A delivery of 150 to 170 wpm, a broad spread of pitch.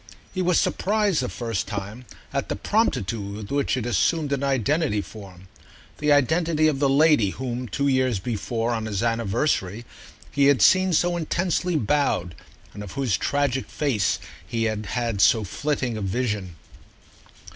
Yes: average, 155 wpm; wide, 5.7 semitones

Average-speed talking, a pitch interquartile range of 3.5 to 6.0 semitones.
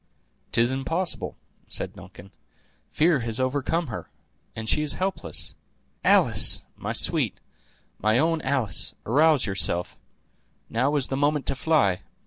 No: slow, 125 wpm; average, 5.2 semitones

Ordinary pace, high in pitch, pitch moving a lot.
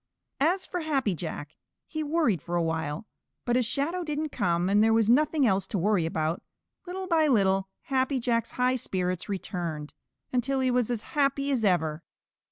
Yes: average, 175 wpm; high, 230 Hz; wide, 7.5 semitones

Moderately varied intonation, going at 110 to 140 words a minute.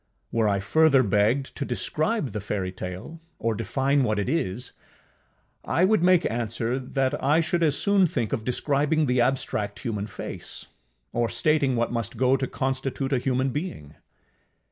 No: average, 4.5 semitones; average, 160 wpm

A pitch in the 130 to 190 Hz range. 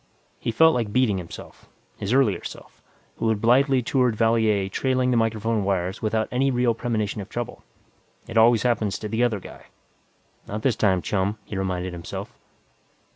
No: low, 110 Hz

